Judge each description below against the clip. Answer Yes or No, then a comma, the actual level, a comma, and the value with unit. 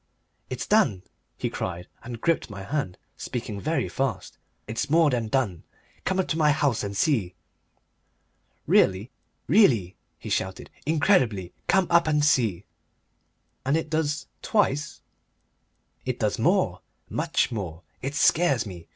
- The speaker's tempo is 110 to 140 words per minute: Yes, slow, 135 wpm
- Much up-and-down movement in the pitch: Yes, wide, 7.7 semitones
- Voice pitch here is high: No, low, 130 Hz